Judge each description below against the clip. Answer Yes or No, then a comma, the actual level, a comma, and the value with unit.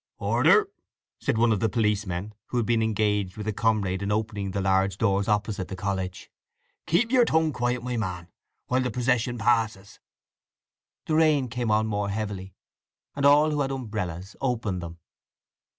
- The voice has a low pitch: Yes, low, 110 Hz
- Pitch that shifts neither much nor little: Yes, average, 3.9 semitones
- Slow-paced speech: No, average, 165 wpm